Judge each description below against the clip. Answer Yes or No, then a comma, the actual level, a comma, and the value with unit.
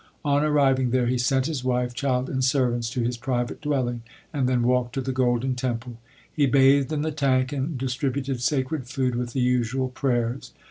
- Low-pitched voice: Yes, low, 130 Hz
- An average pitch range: No, narrow, 1.8 semitones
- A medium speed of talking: Yes, average, 190 wpm